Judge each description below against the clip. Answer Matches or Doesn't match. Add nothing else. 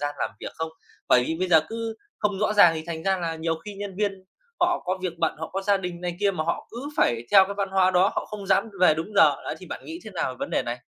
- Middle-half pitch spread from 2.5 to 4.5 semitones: Matches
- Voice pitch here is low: Doesn't match